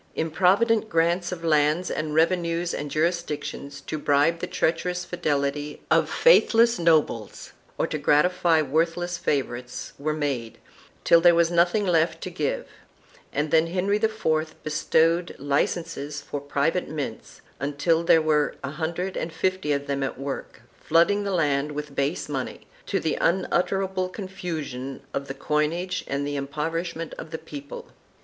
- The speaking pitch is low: No, medium, 160 Hz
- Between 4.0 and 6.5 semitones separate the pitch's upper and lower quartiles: No, average, 3.2 semitones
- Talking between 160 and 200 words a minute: No, average, 145 wpm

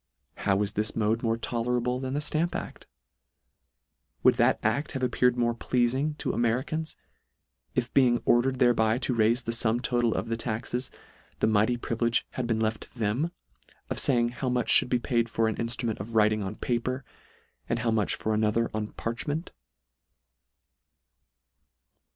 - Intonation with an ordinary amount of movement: No, narrow, 2.1 semitones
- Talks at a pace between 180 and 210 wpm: Yes, average, 185 wpm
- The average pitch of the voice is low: Yes, low, 120 Hz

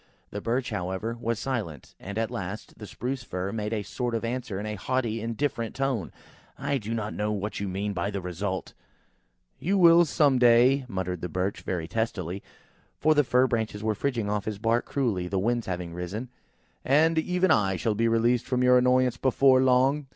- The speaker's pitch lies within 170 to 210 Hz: No, low, 115 Hz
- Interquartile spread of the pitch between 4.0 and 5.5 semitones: Yes, average, 4.3 semitones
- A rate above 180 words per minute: Yes, average, 190 wpm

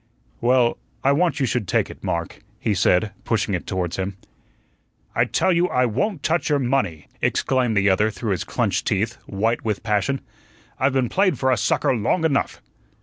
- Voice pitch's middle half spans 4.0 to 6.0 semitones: Yes, average, 5.1 semitones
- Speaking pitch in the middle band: No, low, 120 Hz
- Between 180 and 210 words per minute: Yes, average, 185 wpm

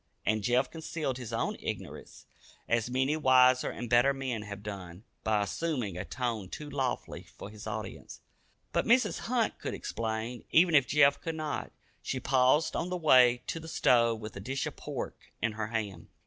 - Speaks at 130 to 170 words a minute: No, average, 180 wpm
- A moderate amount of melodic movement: Yes, average, 4.8 semitones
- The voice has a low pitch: Yes, low, 125 Hz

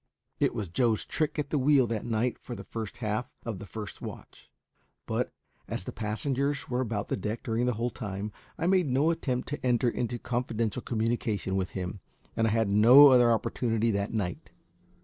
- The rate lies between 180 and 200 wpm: Yes, average, 190 wpm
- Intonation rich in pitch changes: No, average, 2.9 semitones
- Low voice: Yes, low, 115 Hz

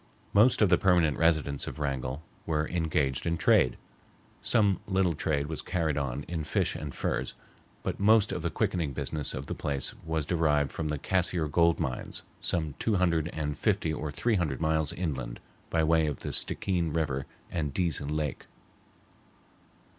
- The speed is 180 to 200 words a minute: No, average, 170 wpm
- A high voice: No, very low, 80 Hz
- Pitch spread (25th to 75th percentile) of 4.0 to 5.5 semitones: No, average, 3.0 semitones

